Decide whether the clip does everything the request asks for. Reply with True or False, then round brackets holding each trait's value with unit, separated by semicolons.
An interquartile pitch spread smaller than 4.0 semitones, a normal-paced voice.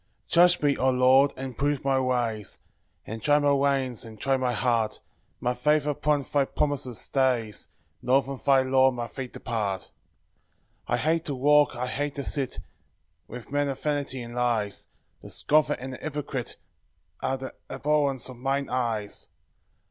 True (2.7 semitones; 170 wpm)